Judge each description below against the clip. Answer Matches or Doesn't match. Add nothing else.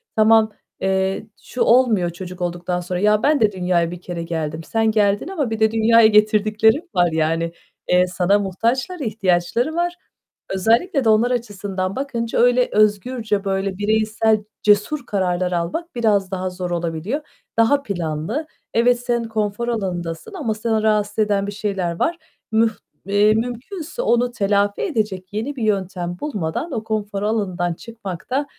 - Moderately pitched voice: Doesn't match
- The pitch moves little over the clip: Doesn't match